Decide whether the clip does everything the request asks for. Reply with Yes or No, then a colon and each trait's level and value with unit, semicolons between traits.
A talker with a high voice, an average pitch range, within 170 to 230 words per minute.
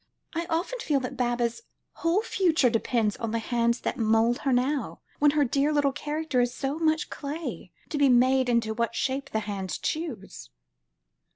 Yes: very high, 265 Hz; average, 4.3 semitones; average, 175 wpm